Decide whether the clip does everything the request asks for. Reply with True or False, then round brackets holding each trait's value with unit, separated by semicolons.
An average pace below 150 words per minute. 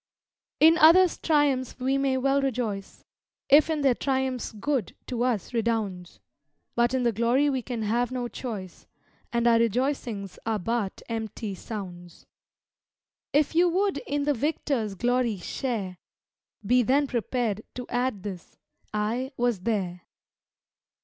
True (140 wpm)